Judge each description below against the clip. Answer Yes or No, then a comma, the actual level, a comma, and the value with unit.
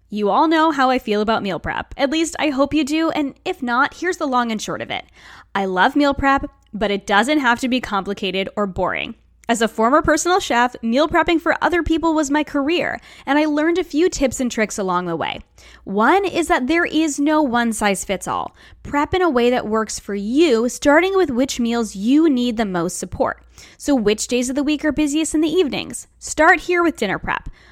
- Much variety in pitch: Yes, wide, 6.0 semitones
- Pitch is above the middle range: Yes, very high, 275 Hz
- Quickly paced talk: Yes, fast, 225 wpm